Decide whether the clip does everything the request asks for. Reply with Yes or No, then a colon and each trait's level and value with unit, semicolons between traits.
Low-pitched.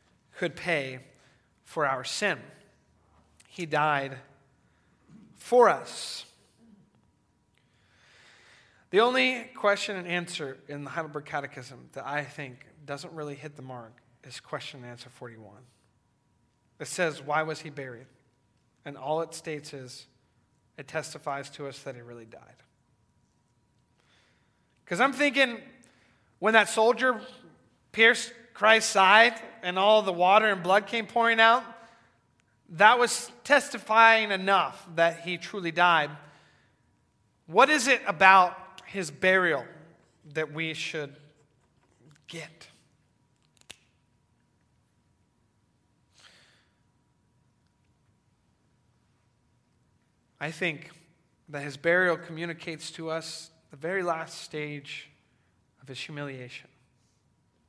No: medium, 155 Hz